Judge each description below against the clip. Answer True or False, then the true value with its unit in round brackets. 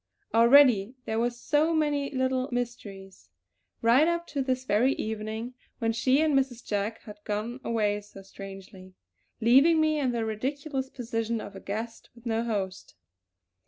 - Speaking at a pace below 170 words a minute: True (155 wpm)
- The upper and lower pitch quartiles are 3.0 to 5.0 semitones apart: True (3.9 semitones)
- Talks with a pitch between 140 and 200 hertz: False (235 Hz)